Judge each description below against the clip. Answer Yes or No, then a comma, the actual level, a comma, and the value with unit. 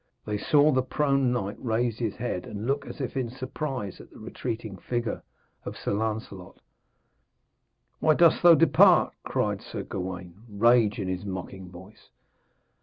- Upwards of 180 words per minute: No, average, 155 wpm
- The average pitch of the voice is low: Yes, low, 115 Hz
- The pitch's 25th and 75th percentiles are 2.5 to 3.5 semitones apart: No, average, 4.8 semitones